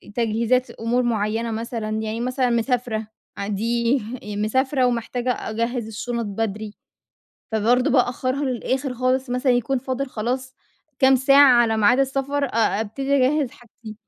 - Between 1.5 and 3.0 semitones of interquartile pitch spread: Yes, average, 2.7 semitones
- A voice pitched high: Yes, high, 245 Hz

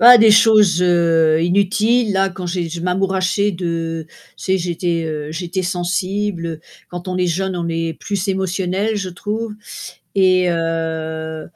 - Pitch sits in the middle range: Yes, medium, 180 Hz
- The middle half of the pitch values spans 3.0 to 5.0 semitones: No, narrow, 2.6 semitones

